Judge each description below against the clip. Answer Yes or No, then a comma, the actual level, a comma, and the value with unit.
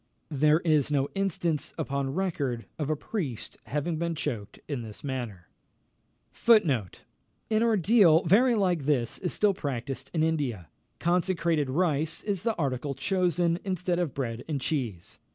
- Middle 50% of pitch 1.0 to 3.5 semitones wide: No, average, 4.9 semitones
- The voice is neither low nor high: Yes, medium, 155 Hz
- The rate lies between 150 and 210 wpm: No, average, 140 wpm